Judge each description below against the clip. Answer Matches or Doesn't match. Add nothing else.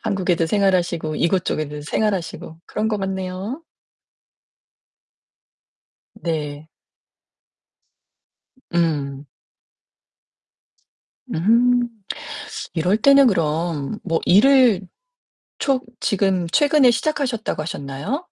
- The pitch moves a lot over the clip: Matches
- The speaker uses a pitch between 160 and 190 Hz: Matches